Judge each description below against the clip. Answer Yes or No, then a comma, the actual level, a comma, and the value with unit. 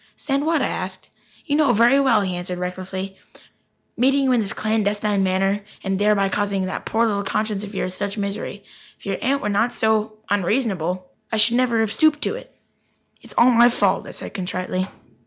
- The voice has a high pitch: Yes, high, 210 Hz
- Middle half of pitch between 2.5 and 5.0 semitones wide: Yes, average, 3.6 semitones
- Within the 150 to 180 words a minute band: No, average, 195 wpm